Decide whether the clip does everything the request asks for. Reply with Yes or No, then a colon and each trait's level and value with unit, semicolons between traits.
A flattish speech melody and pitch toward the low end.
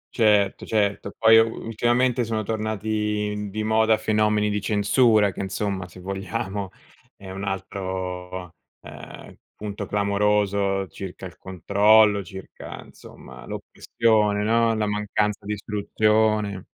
Yes: narrow, 1.8 semitones; low, 105 Hz